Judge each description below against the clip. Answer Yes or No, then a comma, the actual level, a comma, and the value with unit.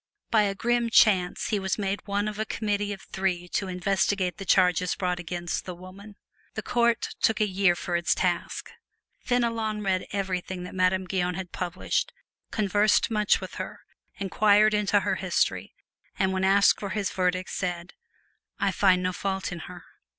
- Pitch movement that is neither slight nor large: No, narrow, 2.2 semitones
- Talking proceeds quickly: No, average, 170 wpm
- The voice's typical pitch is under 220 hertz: Yes, high, 190 Hz